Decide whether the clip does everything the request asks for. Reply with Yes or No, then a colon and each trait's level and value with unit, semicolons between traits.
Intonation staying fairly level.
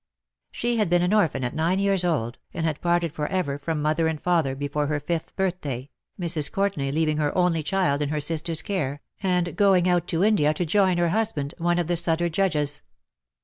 No: average, 3.3 semitones